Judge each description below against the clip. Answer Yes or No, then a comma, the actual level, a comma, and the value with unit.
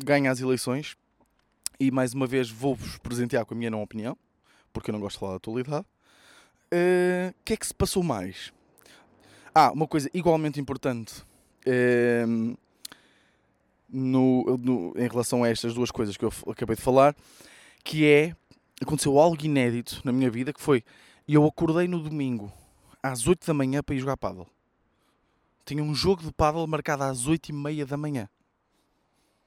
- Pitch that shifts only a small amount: No, average, 4.0 semitones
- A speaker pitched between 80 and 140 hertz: Yes, low, 135 Hz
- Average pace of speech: Yes, average, 170 wpm